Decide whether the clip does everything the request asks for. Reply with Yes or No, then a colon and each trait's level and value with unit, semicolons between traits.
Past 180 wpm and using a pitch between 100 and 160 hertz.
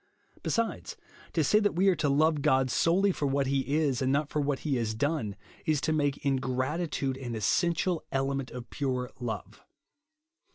No: average, 175 wpm; medium, 140 Hz